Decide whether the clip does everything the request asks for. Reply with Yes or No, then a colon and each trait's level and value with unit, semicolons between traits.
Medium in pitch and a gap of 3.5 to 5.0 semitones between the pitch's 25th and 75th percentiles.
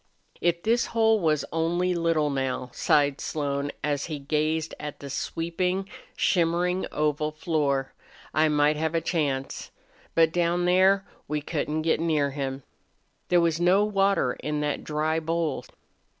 No: medium, 160 Hz; average, 2.9 semitones